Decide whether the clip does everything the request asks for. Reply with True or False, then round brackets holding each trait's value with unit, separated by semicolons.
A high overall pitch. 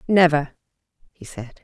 False (150 Hz)